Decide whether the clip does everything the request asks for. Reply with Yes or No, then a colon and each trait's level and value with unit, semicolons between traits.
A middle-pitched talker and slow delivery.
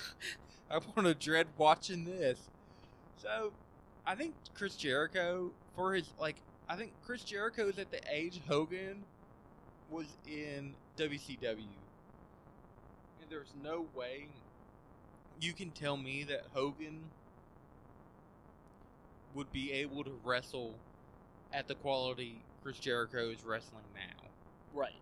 Yes: medium, 150 Hz; slow, 120 wpm